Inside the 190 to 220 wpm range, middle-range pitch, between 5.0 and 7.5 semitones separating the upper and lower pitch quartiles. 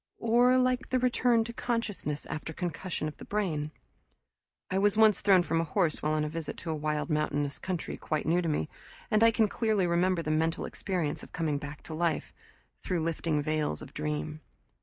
Yes: average, 200 wpm; medium, 165 Hz; wide, 5.5 semitones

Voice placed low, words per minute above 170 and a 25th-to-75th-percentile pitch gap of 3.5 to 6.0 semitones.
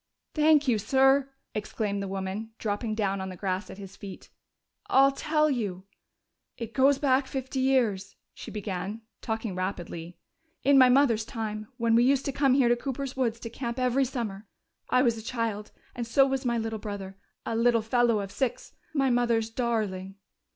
No: high, 230 Hz; average, 180 wpm; average, 4.3 semitones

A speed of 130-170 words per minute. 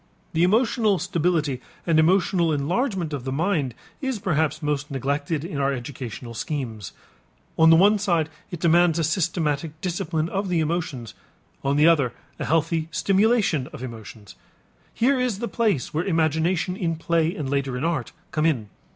Yes: average, 160 wpm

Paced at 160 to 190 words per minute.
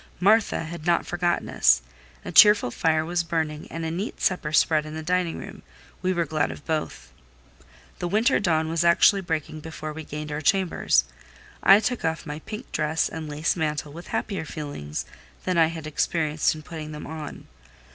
Yes: average, 185 wpm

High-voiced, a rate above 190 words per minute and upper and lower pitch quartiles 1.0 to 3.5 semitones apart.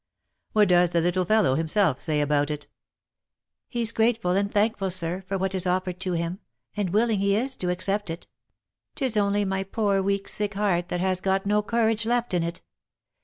Yes: high, 195 Hz; fast, 205 wpm; average, 2.8 semitones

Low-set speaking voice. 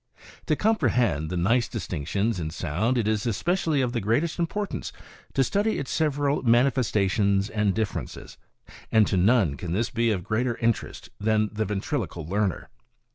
Yes: low, 110 Hz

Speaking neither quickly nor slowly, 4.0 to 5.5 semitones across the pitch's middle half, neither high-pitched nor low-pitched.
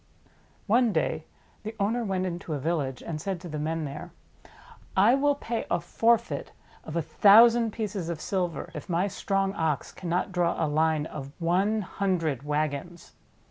Yes: average, 165 wpm; average, 4.6 semitones; medium, 175 Hz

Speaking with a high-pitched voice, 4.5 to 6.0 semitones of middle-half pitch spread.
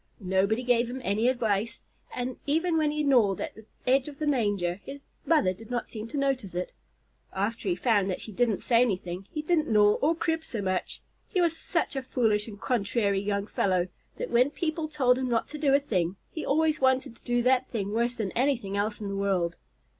Yes: high, 235 Hz; wide, 5.5 semitones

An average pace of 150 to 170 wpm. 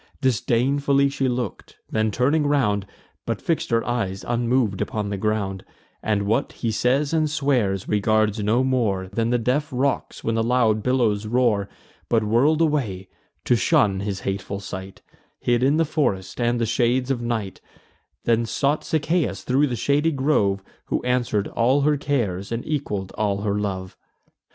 Yes: average, 160 wpm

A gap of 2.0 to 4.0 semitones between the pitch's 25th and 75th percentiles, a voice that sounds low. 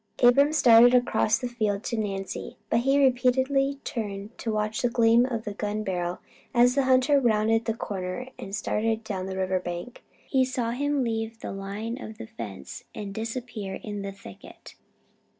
No: average, 3.7 semitones; high, 225 Hz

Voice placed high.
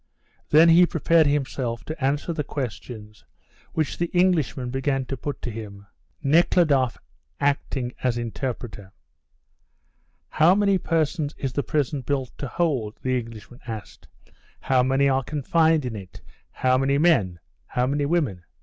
No: low, 135 Hz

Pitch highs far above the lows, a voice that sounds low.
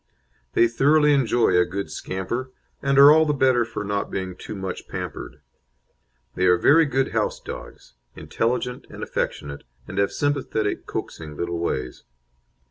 Yes: wide, 6.8 semitones; low, 115 Hz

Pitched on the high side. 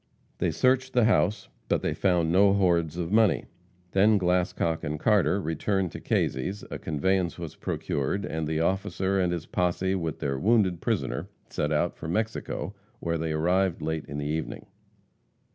No: very low, 90 Hz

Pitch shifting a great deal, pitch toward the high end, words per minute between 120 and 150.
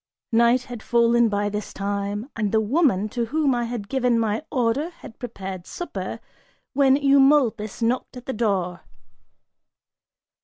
No: average, 3.8 semitones; high, 235 Hz; average, 145 wpm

